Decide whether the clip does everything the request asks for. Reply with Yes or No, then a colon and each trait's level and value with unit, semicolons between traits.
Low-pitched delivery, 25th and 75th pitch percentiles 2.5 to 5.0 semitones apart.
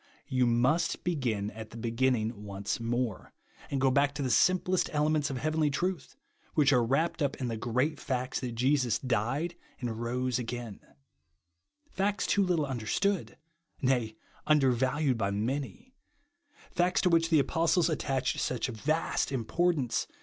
Yes: low, 130 Hz; average, 4.7 semitones